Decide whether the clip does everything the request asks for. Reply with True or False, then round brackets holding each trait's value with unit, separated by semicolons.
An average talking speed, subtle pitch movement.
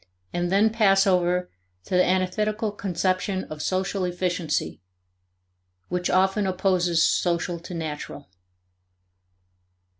False (110 wpm; 1.8 semitones)